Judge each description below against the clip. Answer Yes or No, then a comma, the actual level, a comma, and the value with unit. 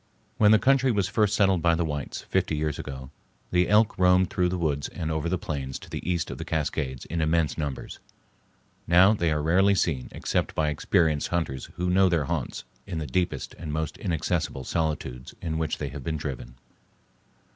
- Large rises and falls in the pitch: No, average, 3.4 semitones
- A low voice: Yes, very low, 80 Hz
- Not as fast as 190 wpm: No, average, 195 wpm